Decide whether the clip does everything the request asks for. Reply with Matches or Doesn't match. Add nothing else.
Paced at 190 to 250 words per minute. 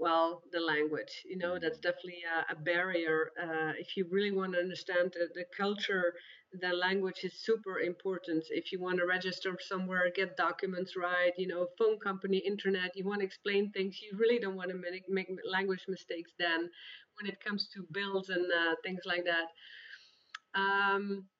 Doesn't match